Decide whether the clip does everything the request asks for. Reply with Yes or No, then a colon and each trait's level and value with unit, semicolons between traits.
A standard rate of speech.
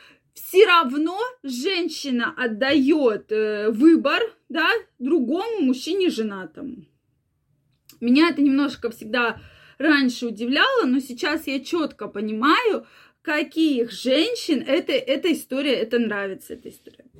No: slow, 100 wpm